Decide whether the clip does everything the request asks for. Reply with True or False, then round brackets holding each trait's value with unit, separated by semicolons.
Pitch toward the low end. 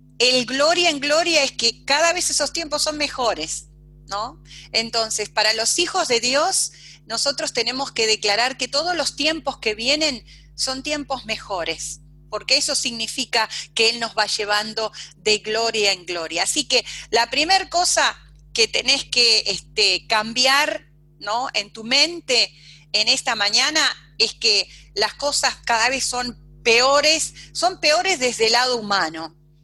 False (230 Hz)